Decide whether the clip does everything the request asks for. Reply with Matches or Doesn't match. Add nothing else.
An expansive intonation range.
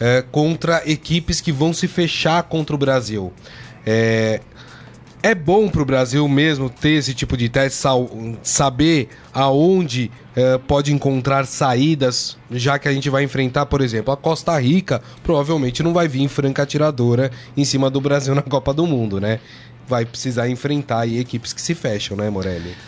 Doesn't match